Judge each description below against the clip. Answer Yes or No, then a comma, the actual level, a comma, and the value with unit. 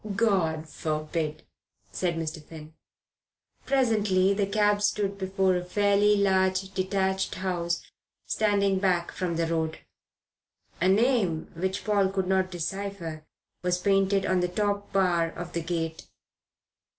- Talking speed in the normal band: No, slow, 125 wpm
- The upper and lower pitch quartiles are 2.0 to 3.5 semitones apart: Yes, average, 2.8 semitones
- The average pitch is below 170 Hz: No, high, 190 Hz